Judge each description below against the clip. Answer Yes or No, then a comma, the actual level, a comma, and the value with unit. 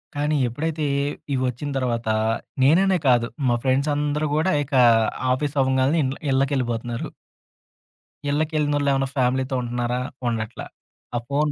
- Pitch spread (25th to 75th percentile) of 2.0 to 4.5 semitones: Yes, average, 3.1 semitones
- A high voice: No, low, 135 Hz